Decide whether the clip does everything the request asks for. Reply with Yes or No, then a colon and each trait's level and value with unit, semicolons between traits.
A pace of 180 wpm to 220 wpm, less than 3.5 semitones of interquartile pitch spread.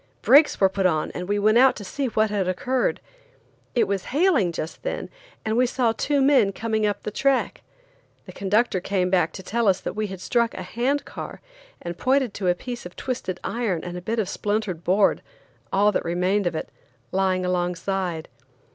No: average, 190 wpm; average, 4.5 semitones